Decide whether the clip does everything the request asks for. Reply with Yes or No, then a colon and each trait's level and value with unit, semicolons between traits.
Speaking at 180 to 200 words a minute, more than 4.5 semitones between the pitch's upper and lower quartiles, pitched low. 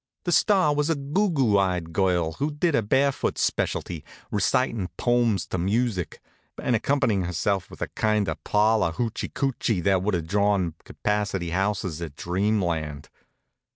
No: average, 150 wpm; wide, 5.4 semitones; low, 105 Hz